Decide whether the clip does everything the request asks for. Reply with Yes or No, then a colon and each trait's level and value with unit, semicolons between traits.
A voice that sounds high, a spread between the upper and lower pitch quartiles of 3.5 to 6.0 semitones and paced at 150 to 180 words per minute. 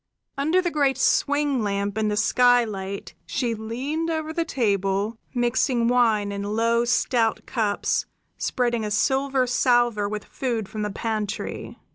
No: high, 235 Hz; average, 3.9 semitones; average, 140 wpm